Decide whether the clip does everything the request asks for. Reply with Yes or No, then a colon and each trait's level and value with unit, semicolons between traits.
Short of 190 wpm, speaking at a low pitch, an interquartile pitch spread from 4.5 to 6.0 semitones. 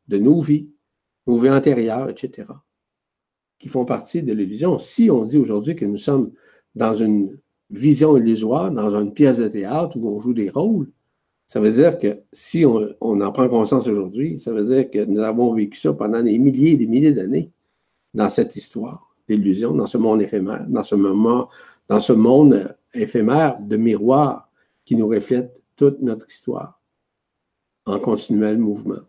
Yes: average, 175 wpm; low, 115 Hz; average, 5.0 semitones